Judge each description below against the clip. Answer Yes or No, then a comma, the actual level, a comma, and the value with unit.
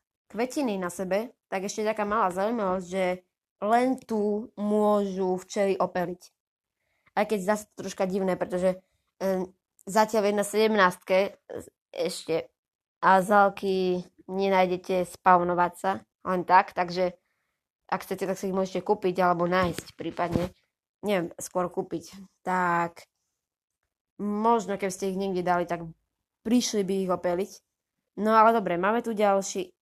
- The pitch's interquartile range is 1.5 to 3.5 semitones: Yes, narrow, 2.4 semitones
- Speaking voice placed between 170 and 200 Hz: Yes, high, 190 Hz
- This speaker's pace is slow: No, average, 135 wpm